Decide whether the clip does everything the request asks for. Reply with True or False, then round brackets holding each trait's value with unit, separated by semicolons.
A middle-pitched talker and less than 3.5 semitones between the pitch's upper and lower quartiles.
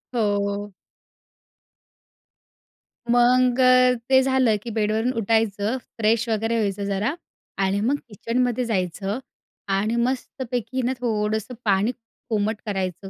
False (220 Hz; 3.1 semitones)